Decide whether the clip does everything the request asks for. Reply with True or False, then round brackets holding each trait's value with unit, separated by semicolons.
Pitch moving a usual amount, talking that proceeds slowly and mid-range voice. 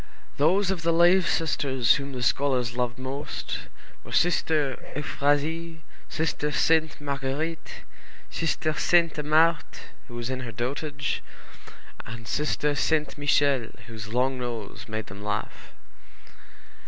True (4.3 semitones; 120 wpm; 145 Hz)